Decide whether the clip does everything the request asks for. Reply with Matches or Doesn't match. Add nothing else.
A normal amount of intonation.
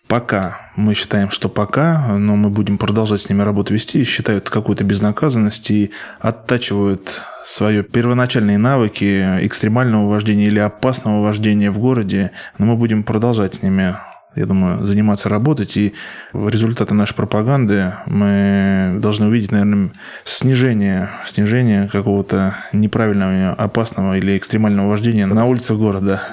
Doesn't match